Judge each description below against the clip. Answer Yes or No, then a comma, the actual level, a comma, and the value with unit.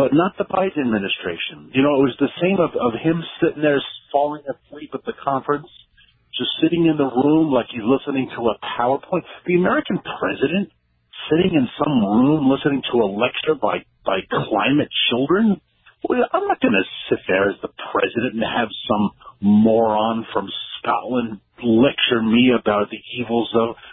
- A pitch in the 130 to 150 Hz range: Yes, low, 135 Hz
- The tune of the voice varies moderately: No, wide, 6.0 semitones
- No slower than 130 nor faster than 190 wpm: Yes, average, 170 wpm